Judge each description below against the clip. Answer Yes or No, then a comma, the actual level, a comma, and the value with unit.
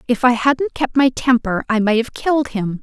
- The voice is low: No, high, 245 Hz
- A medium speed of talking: No, fast, 235 wpm